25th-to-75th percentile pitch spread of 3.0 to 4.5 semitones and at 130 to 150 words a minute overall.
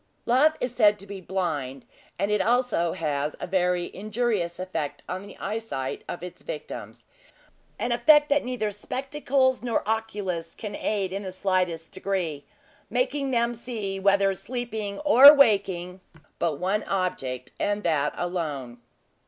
No: average, 5.2 semitones; average, 145 wpm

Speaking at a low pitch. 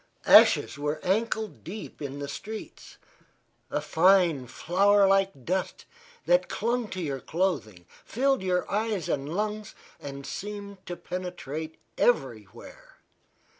No: medium, 185 Hz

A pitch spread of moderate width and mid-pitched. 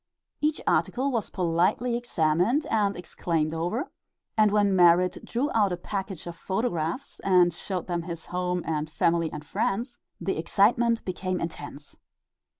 Yes: average, 4.7 semitones; medium, 180 Hz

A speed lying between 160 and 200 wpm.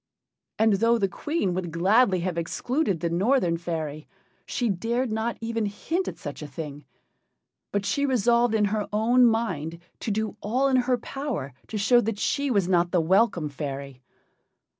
Yes: average, 170 wpm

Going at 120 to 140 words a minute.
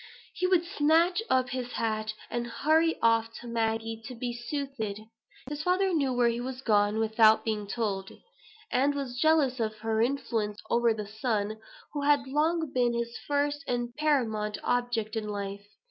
No: average, 165 wpm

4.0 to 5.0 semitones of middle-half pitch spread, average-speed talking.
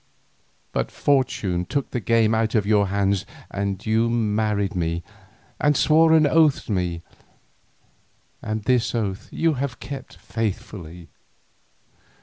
No: average, 4.5 semitones; slow, 130 wpm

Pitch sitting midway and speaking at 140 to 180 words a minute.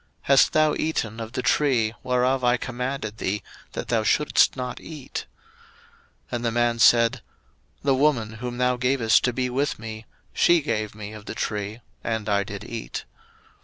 No: low, 120 Hz; average, 170 wpm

